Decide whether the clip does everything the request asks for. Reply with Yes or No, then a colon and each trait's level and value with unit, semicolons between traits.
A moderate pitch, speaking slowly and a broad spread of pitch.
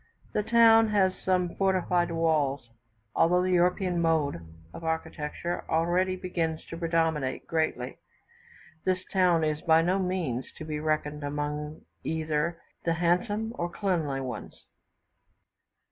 No: medium, 165 Hz; slow, 125 wpm; average, 3.1 semitones